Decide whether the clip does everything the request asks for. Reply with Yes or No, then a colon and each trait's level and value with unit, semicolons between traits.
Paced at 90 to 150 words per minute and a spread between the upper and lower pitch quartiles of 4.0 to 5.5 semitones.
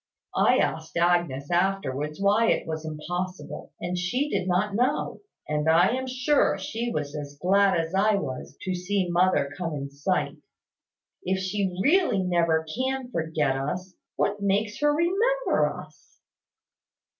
Yes: average, 145 wpm; average, 4.6 semitones